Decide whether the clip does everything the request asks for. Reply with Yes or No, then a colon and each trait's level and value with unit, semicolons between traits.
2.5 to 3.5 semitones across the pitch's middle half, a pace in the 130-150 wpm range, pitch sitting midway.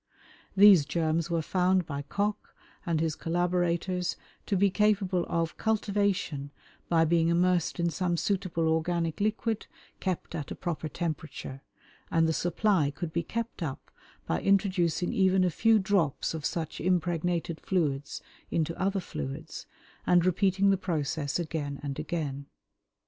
Yes: average, 2.9 semitones; average, 140 wpm; medium, 170 Hz